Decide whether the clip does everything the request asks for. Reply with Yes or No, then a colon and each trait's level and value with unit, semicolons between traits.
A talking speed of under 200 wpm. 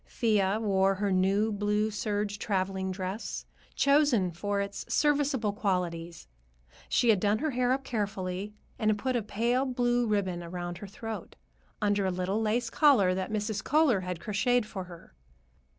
Yes: average, 160 wpm